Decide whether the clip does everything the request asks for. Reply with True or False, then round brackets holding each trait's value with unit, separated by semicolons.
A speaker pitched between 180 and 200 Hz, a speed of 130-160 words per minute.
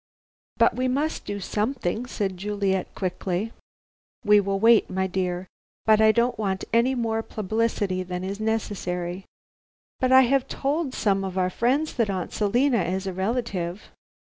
False (210 Hz; 150 wpm)